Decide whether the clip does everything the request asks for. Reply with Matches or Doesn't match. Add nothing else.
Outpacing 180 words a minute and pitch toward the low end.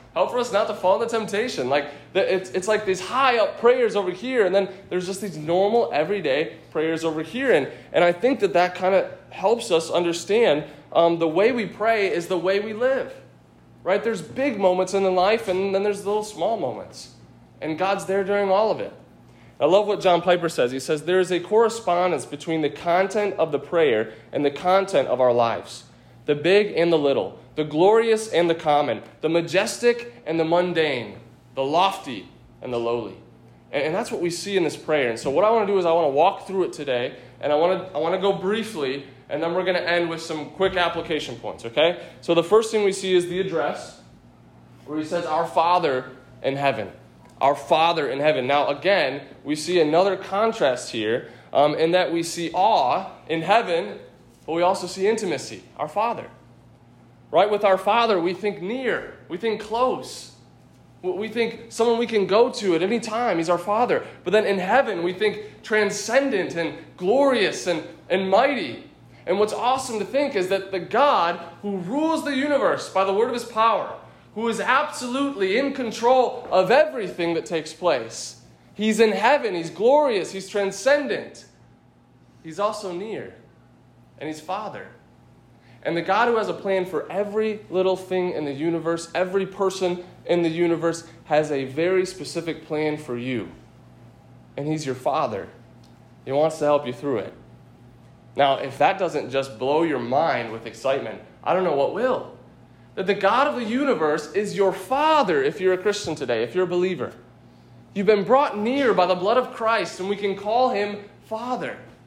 Doesn't match